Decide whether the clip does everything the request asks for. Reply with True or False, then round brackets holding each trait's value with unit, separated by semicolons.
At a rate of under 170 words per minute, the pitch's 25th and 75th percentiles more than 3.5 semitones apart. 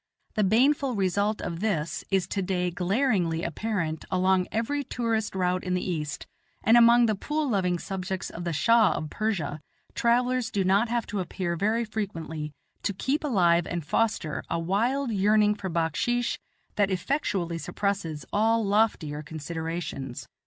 True (150 wpm; 4.8 semitones)